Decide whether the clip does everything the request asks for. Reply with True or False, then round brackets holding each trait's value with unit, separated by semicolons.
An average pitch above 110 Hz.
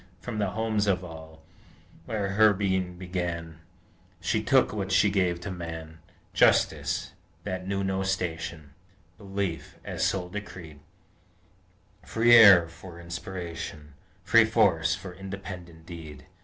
False (95 Hz)